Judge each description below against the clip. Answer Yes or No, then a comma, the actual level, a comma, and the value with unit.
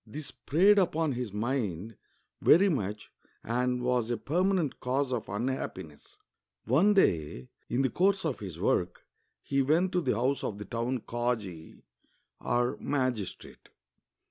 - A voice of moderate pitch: No, low, 125 Hz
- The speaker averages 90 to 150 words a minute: Yes, average, 140 wpm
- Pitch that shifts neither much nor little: No, wide, 5.8 semitones